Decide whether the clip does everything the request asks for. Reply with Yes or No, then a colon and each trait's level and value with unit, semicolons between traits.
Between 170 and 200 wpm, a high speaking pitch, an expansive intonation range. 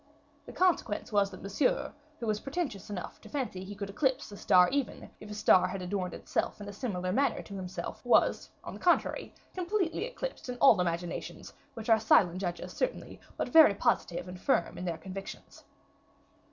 Yes: average, 185 wpm; high, 205 Hz; wide, 6.4 semitones